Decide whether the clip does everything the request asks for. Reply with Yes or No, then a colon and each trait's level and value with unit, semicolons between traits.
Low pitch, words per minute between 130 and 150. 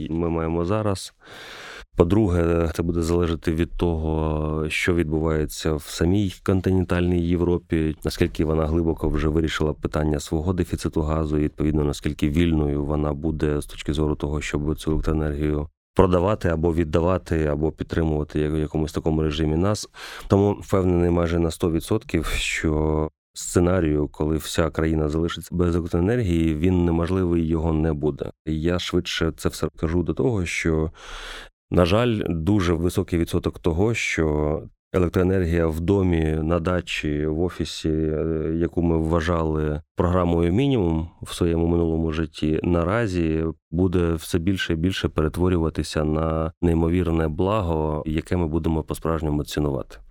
Yes: very low, 80 Hz; average, 135 wpm